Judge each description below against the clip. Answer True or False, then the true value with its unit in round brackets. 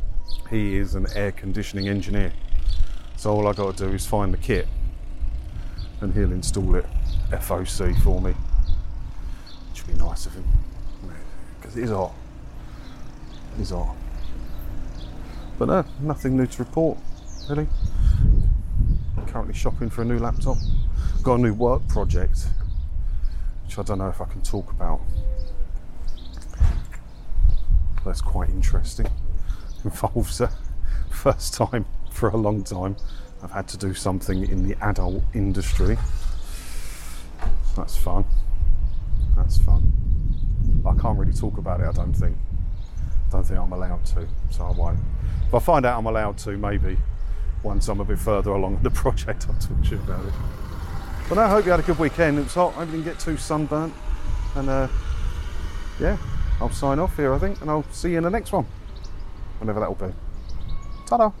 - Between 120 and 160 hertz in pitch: False (95 Hz)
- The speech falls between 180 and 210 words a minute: False (160 wpm)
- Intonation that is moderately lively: True (4.6 semitones)